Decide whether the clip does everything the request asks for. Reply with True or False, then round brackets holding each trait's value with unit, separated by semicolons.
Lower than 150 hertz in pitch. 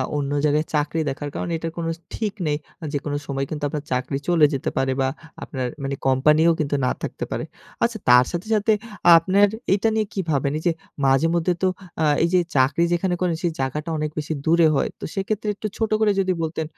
False (160 Hz)